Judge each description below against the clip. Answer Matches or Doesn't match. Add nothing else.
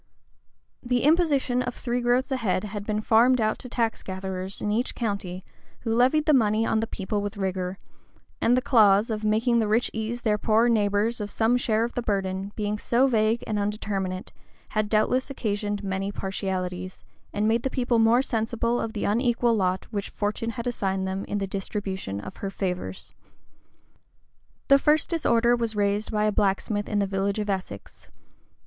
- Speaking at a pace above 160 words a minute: Matches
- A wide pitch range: Doesn't match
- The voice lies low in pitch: Doesn't match